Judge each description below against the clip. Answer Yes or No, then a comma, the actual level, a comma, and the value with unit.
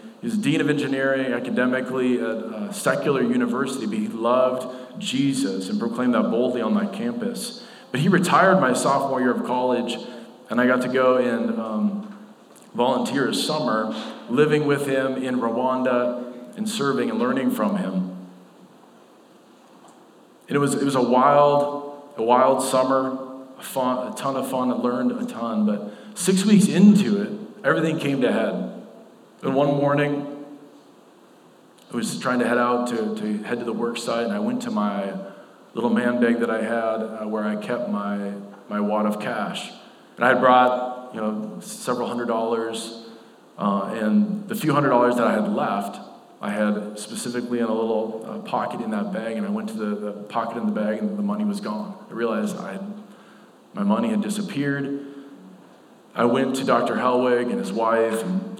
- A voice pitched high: No, low, 130 Hz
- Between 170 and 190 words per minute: Yes, average, 180 wpm